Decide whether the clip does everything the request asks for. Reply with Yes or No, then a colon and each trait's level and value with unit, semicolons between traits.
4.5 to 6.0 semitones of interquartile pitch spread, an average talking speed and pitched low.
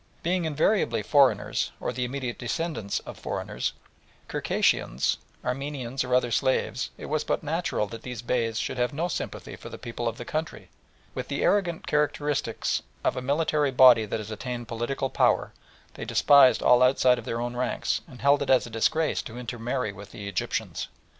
No: average, 3.5 semitones; average, 175 wpm; low, 125 Hz